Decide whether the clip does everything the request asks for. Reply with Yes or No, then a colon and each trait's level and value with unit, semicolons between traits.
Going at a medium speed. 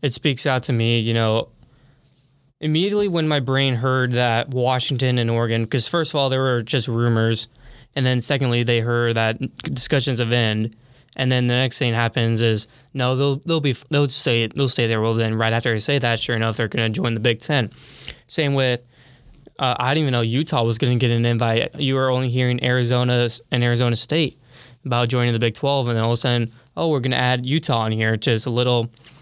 No: fast, 225 wpm